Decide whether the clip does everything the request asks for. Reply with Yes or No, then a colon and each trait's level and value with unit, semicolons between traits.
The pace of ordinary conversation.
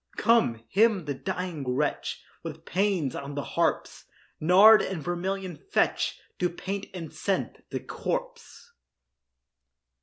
No: slow, 120 wpm